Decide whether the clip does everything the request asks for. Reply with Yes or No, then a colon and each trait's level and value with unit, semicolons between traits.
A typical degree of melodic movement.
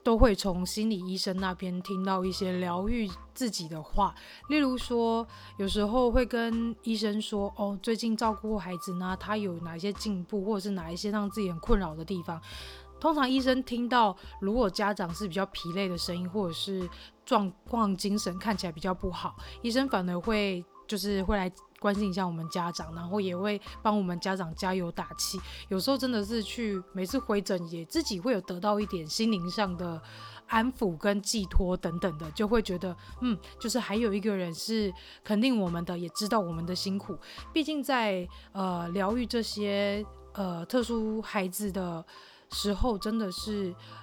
Yes: average, 3.3 semitones